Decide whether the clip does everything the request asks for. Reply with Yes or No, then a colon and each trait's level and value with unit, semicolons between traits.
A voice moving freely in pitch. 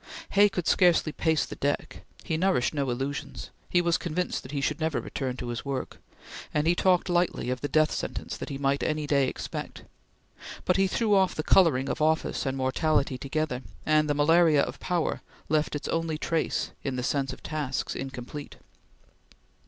No: average, 3.4 semitones